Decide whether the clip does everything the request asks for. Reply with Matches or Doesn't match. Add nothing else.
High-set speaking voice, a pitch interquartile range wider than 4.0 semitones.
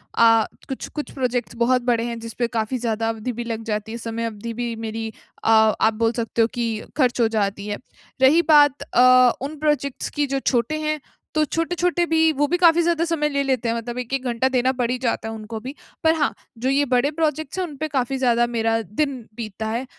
Matches